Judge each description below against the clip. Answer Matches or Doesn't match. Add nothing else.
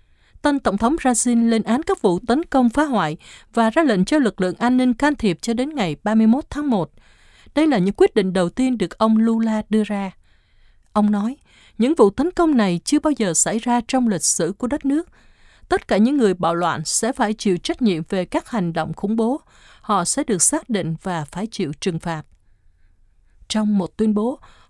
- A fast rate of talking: Doesn't match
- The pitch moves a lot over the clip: Matches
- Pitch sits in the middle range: Doesn't match